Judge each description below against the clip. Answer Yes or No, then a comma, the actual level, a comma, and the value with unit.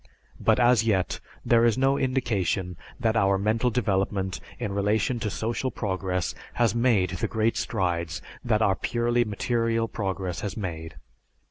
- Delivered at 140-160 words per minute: Yes, average, 145 wpm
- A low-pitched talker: Yes, low, 105 Hz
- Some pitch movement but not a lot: Yes, average, 3.7 semitones